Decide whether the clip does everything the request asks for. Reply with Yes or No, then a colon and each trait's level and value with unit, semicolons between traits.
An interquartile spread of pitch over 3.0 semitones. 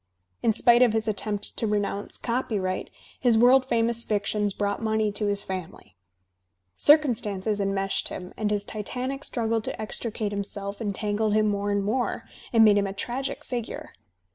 No: narrow, 2.4 semitones